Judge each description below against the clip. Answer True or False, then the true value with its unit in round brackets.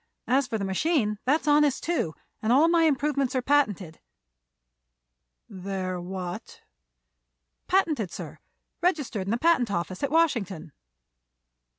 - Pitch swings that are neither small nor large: False (7.8 semitones)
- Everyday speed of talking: False (120 wpm)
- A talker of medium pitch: False (250 Hz)